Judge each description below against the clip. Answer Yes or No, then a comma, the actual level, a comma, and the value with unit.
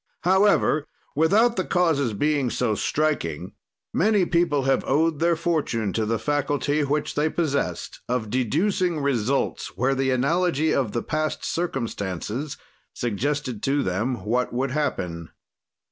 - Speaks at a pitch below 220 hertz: Yes, medium, 140 Hz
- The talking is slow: Yes, slow, 130 wpm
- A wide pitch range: No, average, 4.8 semitones